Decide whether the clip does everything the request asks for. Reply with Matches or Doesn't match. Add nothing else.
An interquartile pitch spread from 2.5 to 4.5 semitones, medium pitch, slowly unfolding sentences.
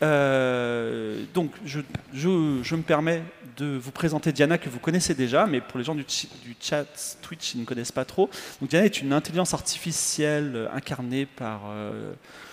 Doesn't match